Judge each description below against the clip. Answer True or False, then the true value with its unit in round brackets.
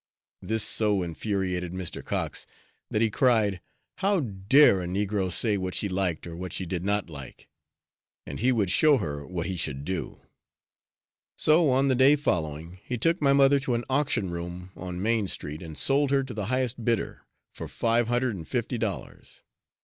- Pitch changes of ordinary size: False (6.2 semitones)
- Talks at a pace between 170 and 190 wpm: True (180 wpm)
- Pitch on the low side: True (105 Hz)